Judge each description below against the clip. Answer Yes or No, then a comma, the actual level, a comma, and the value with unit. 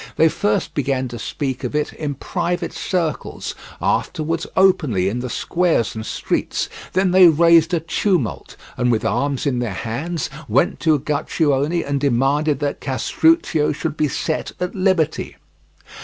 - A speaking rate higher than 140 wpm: Yes, average, 150 wpm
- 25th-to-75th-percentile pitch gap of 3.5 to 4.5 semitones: Yes, average, 4.2 semitones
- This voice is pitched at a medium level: Yes, medium, 150 Hz